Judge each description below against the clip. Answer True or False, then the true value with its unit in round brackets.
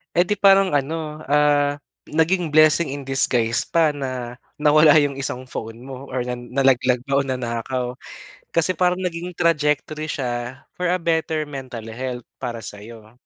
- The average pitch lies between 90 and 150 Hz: True (140 Hz)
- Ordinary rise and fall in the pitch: True (3.9 semitones)